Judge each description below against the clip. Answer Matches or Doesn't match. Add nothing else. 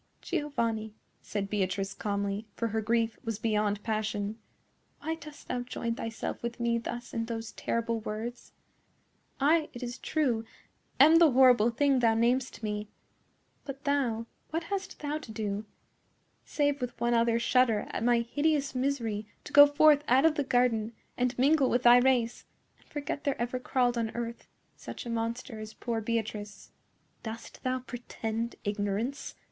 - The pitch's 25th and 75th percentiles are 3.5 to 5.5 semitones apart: Doesn't match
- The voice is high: Matches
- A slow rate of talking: Doesn't match